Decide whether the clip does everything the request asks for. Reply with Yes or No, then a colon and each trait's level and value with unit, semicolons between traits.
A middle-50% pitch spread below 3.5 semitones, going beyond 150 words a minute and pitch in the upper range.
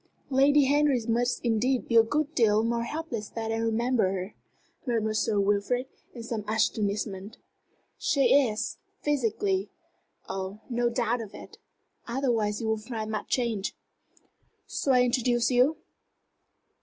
No: average, 2.8 semitones; slow, 135 wpm; high, 235 Hz